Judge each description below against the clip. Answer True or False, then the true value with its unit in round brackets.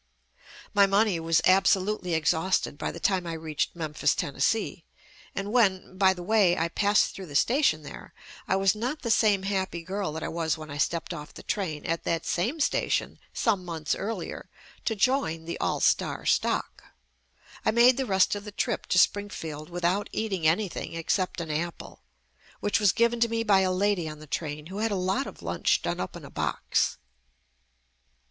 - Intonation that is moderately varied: True (4.0 semitones)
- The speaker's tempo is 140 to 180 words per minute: False (190 wpm)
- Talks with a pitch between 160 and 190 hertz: True (185 Hz)